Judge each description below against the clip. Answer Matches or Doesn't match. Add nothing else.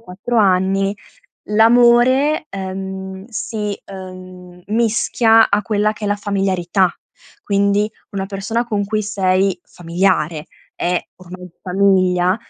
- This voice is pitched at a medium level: Doesn't match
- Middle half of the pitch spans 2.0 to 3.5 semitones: Matches